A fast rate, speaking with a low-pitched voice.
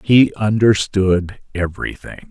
No: slow, 80 wpm; very low, 95 Hz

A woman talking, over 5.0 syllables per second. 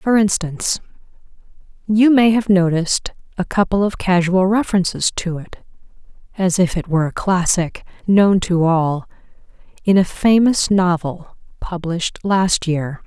No: female; 4.5 syllables/s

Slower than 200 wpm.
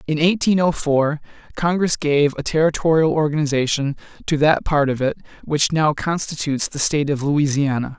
Yes: average, 160 wpm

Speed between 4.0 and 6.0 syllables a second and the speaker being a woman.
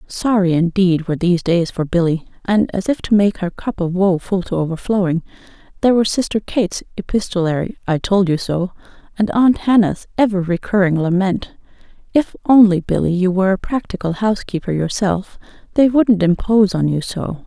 Yes: 5.5 syllables/s; female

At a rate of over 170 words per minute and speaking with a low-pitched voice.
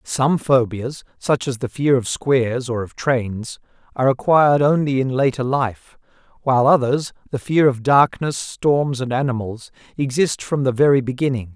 No: average, 160 wpm; low, 130 Hz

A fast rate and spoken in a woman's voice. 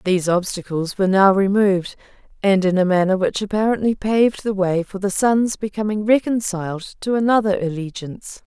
No: average, 155 wpm; female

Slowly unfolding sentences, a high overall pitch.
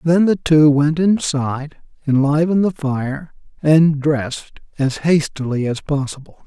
No: slow, 130 wpm; medium, 150 Hz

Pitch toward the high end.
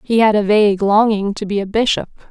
Yes: high, 210 Hz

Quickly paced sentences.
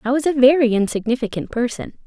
No: average, 175 wpm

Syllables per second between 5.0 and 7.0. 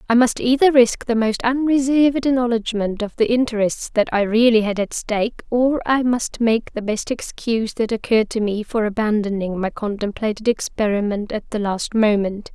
Yes: 5.1 syllables/s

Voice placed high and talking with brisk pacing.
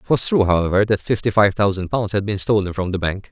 No: low, 100 Hz; fast, 270 wpm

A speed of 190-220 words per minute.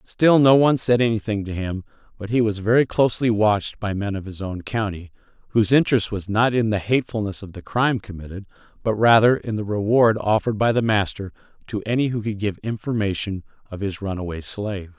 Yes: average, 195 wpm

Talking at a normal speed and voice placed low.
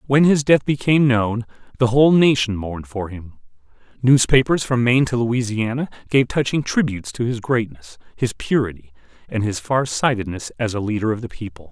Yes: average, 175 wpm; low, 115 Hz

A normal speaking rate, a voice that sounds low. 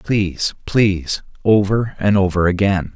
No: slow, 120 wpm; very low, 95 Hz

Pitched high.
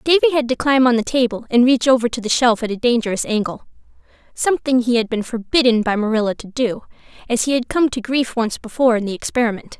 Yes: high, 240 Hz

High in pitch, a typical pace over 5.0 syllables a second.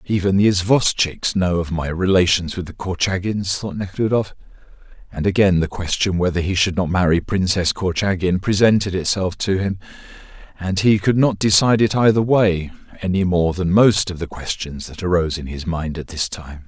No: very low, 90 Hz; 5.2 syllables/s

